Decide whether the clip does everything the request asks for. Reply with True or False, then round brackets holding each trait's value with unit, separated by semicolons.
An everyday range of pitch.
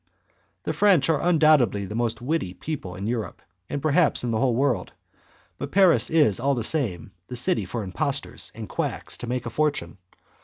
False (6.0 semitones)